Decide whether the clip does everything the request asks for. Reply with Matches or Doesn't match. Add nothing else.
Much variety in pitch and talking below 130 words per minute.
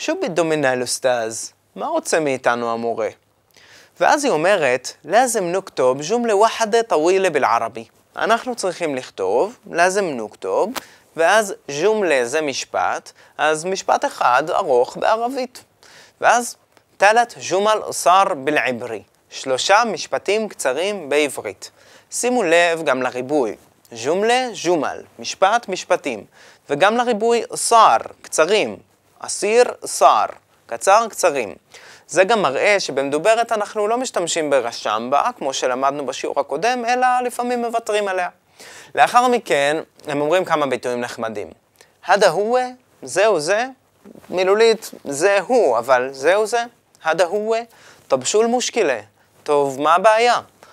Matches